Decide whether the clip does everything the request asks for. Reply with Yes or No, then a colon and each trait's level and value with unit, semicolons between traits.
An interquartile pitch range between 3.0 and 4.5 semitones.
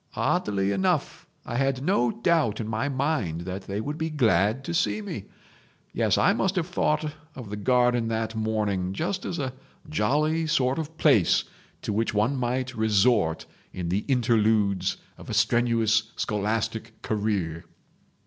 No: wide, 5.5 semitones